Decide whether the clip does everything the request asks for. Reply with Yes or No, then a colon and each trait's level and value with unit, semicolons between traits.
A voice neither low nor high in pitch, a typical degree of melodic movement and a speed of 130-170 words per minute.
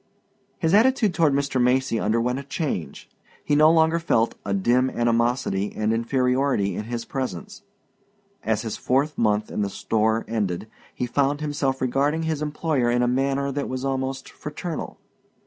No: low, 130 Hz; average, 4.1 semitones; average, 160 wpm